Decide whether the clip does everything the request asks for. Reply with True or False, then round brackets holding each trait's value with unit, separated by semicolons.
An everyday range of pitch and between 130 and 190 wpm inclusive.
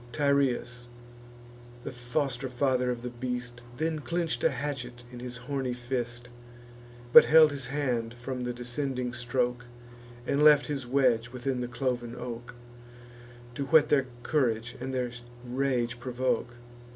False (2.1 semitones; 140 wpm)